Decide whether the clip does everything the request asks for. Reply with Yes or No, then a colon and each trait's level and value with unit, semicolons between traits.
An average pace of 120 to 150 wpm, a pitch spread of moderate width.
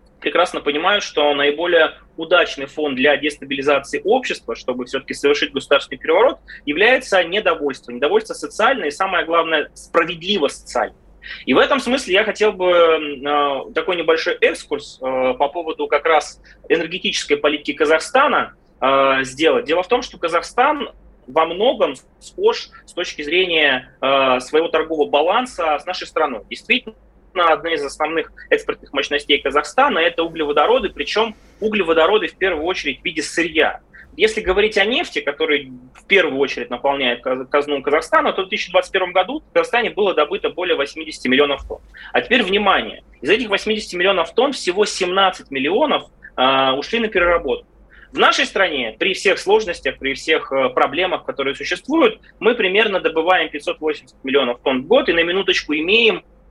No: average, 145 wpm; wide, 6.4 semitones